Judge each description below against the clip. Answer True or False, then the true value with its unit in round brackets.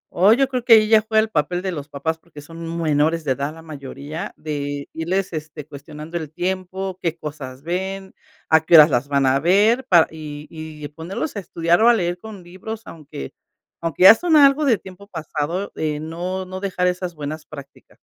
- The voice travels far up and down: False (4.0 semitones)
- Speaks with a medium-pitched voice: True (165 Hz)